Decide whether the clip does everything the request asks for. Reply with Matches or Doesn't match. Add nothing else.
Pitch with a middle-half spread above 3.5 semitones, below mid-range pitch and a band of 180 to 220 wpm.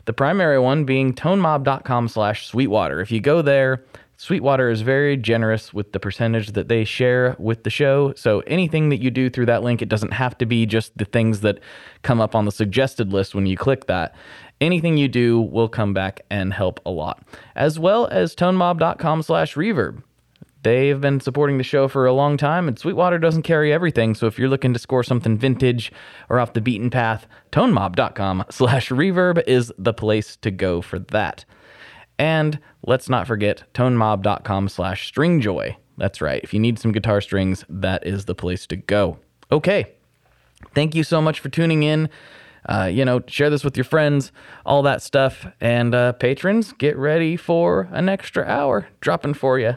Matches